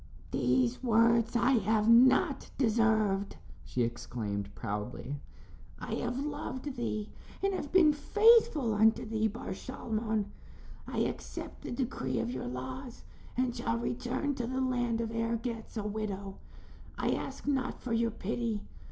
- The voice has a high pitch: Yes, high, 230 Hz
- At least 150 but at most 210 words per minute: No, average, 140 wpm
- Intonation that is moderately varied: Yes, average, 3.9 semitones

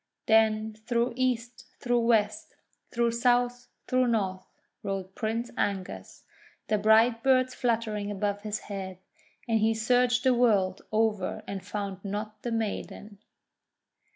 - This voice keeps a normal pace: No, slow, 125 wpm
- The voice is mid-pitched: No, high, 220 Hz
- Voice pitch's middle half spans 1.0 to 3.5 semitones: Yes, average, 2.8 semitones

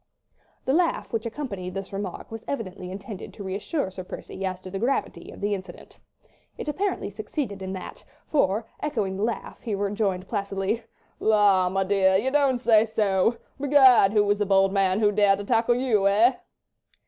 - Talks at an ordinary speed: Yes, average, 170 wpm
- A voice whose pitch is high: Yes, high, 205 Hz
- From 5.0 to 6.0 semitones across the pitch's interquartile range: No, average, 3.3 semitones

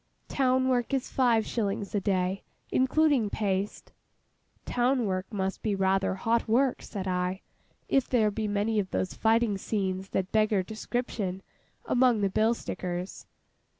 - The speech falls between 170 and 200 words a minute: No, average, 145 wpm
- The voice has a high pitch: Yes, high, 210 Hz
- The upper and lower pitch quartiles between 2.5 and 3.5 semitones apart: No, average, 3.9 semitones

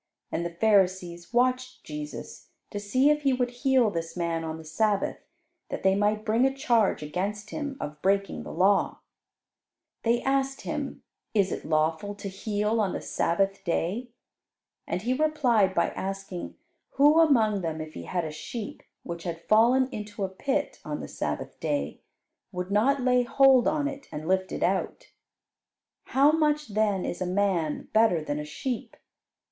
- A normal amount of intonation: No, wide, 6.1 semitones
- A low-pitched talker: No, high, 205 Hz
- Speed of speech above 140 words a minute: Yes, average, 170 wpm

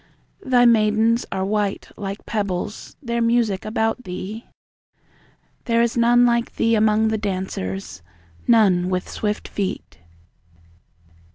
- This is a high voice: Yes, high, 215 Hz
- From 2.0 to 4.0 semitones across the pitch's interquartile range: Yes, average, 3.5 semitones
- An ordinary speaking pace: No, slow, 100 wpm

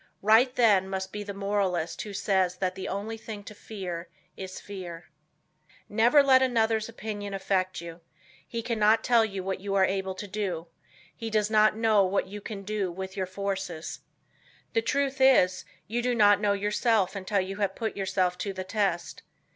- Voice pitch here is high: Yes, high, 200 Hz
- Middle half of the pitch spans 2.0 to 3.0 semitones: Yes, average, 2.7 semitones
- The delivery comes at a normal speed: Yes, average, 175 wpm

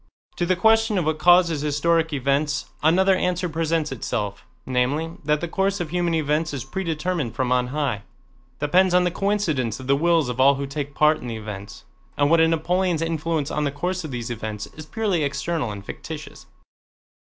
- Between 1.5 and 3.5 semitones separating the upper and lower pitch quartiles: No, average, 4.3 semitones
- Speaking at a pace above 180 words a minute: Yes, average, 190 wpm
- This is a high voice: No, medium, 155 Hz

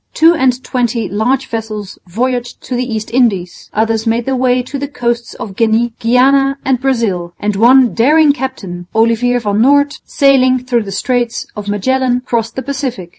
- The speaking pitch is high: Yes, high, 245 Hz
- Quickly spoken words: No, average, 175 wpm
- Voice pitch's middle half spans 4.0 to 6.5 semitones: No, average, 2.8 semitones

